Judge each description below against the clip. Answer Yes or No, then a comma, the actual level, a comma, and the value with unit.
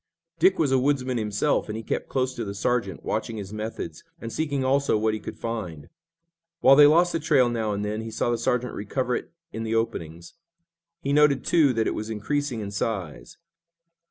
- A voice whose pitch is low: Yes, low, 115 Hz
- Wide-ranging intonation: No, average, 4.2 semitones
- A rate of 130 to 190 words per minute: No, fast, 205 wpm